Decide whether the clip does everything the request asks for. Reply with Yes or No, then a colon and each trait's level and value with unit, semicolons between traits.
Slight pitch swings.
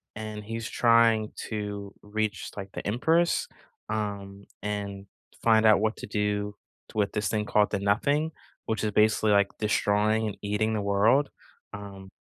Yes: narrow, 1.3 semitones